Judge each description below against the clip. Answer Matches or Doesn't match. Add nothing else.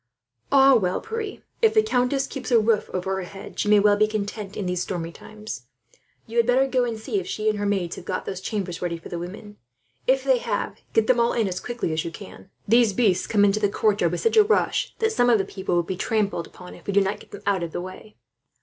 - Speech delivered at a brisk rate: Matches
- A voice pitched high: Matches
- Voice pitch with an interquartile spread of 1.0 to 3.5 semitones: Doesn't match